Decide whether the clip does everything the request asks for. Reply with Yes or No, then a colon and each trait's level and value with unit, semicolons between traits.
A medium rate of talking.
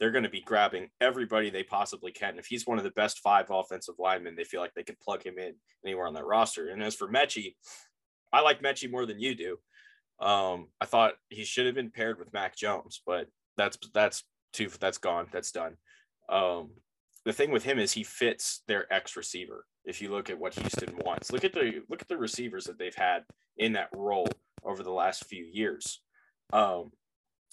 No: fast, 215 wpm